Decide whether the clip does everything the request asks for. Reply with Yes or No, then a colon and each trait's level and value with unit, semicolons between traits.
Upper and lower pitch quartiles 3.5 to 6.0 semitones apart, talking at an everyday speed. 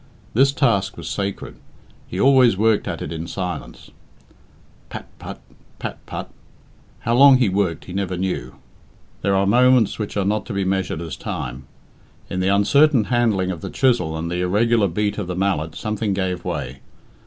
Yes: average, 4.0 semitones; average, 175 wpm